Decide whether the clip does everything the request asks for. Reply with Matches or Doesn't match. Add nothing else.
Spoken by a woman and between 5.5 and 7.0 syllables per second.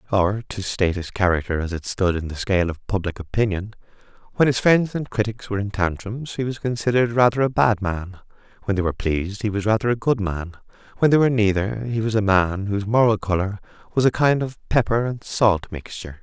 Doesn't match